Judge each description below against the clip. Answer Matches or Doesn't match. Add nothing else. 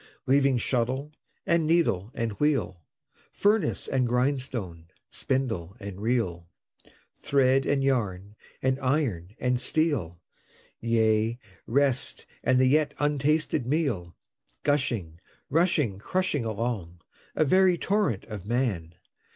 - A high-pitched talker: Doesn't match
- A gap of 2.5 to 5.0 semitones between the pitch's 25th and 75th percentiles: Doesn't match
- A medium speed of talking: Doesn't match